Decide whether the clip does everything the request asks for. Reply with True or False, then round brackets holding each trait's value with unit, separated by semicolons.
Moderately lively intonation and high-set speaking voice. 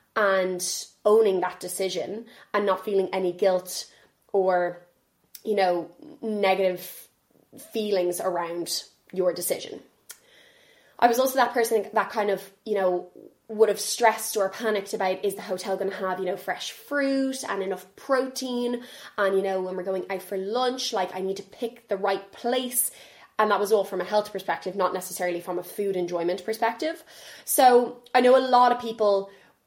True (4.3 semitones; 200 Hz)